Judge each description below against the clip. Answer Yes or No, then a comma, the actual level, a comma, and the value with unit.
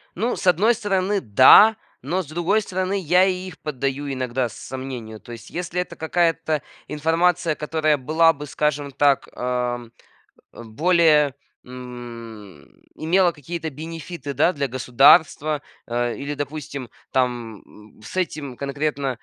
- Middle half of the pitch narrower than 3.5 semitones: No, average, 5.2 semitones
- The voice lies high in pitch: No, medium, 145 Hz